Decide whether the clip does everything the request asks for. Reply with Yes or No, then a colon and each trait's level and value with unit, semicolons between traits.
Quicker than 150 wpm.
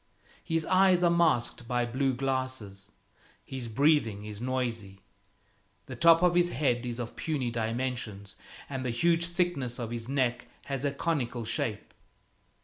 No: average, 145 wpm